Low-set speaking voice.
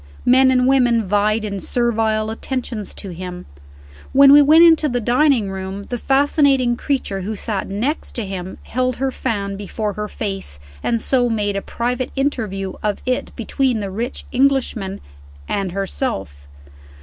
No: high, 225 Hz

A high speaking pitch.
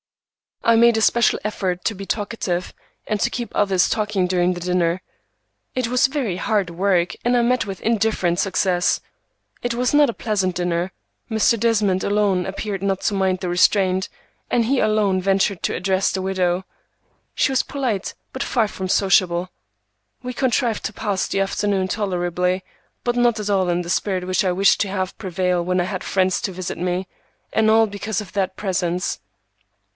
Yes: high, 195 Hz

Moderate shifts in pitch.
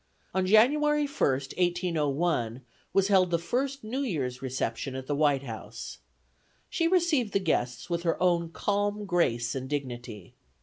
No: wide, 7.8 semitones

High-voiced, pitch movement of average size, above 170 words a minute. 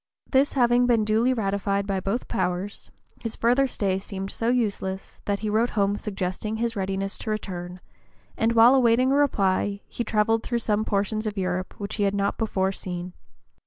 Yes: high, 210 Hz; average, 3.0 semitones; average, 185 wpm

